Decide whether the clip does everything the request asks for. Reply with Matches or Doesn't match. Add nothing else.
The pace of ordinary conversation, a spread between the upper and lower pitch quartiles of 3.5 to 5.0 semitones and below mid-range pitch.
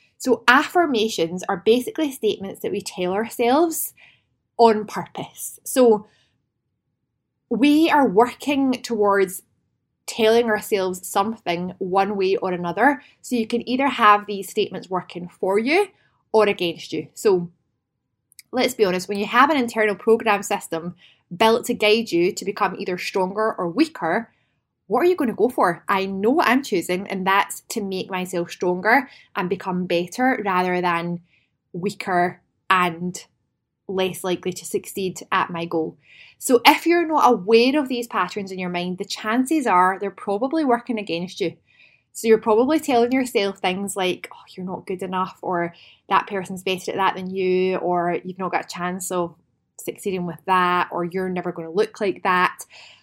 Doesn't match